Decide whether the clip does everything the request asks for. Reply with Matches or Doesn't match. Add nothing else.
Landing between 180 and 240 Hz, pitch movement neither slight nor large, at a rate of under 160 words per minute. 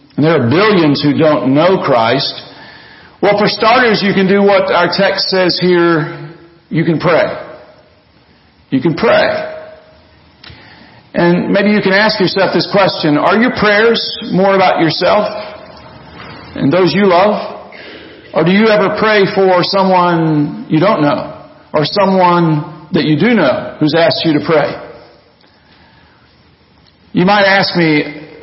Matches